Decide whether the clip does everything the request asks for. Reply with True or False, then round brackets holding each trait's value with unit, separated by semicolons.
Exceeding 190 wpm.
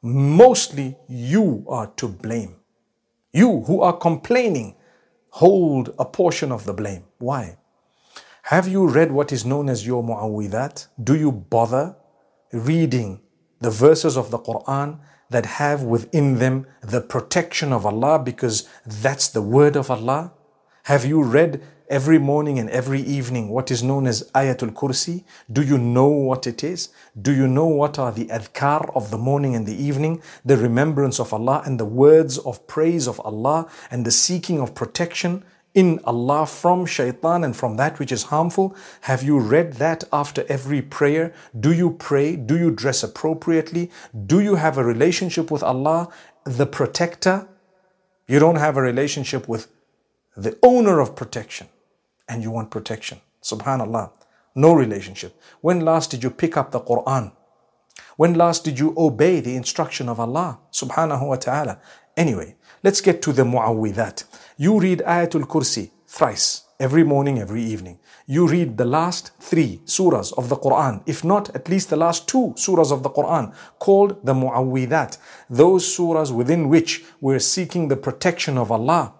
False (165 wpm)